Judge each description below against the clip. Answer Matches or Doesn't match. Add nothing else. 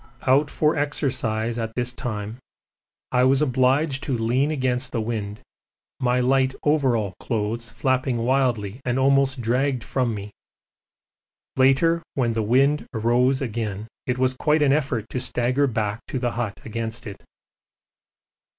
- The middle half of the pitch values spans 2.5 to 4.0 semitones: Matches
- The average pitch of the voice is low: Matches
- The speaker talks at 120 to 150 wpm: Matches